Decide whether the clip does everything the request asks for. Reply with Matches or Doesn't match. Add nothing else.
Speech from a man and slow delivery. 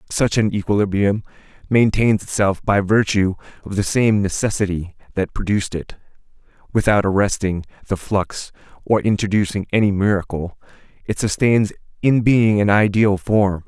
Matches